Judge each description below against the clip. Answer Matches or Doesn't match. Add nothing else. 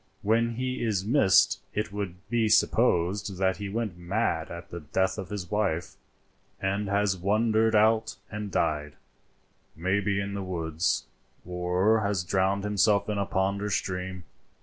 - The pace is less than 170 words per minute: Matches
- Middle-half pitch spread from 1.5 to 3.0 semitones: Matches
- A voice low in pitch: Matches